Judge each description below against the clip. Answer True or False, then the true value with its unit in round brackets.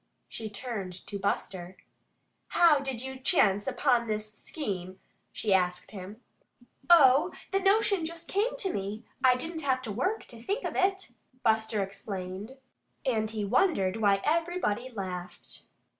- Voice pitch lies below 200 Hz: False (230 Hz)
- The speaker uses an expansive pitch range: True (8.2 semitones)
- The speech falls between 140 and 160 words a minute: True (145 wpm)